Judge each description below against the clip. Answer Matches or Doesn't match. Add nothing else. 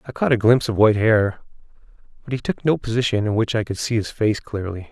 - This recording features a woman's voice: Doesn't match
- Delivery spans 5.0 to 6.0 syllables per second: Doesn't match